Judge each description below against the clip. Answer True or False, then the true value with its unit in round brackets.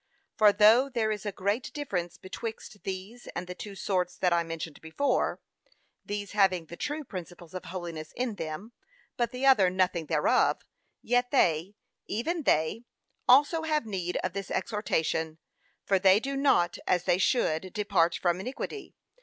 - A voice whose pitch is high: True (195 Hz)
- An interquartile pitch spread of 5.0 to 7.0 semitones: True (5.4 semitones)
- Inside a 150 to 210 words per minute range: True (160 wpm)